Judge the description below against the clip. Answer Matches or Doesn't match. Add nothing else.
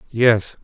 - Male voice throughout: Matches